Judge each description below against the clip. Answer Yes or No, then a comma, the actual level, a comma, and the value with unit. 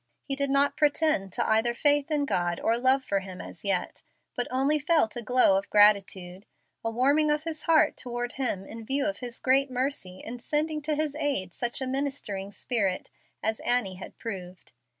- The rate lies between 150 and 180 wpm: No, average, 190 wpm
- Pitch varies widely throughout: Yes, wide, 6.2 semitones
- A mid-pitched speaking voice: No, high, 245 Hz